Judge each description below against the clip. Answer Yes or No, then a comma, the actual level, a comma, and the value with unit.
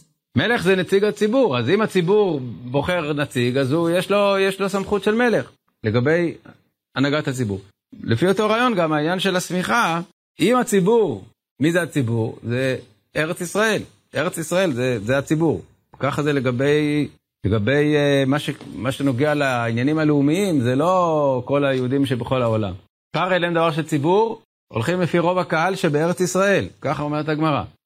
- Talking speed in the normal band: No, fast, 155 wpm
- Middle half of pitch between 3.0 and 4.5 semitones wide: No, average, 5.1 semitones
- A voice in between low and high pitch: Yes, medium, 150 Hz